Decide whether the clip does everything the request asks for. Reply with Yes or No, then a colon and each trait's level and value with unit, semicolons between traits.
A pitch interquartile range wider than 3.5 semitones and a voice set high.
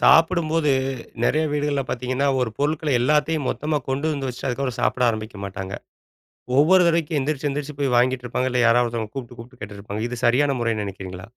No: average, 4.0 semitones; low, 130 Hz